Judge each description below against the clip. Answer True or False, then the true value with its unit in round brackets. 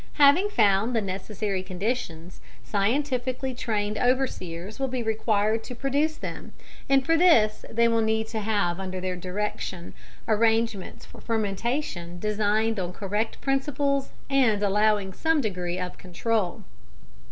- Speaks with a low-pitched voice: False (220 Hz)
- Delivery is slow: True (130 wpm)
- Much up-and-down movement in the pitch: False (4.7 semitones)